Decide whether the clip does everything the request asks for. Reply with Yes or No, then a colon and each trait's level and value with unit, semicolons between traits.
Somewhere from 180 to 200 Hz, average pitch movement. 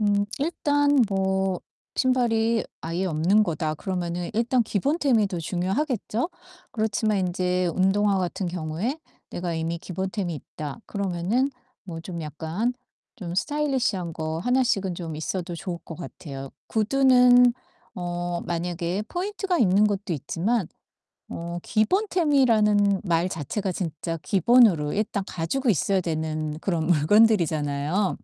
Yes: high, 190 Hz; average, 5.0 semitones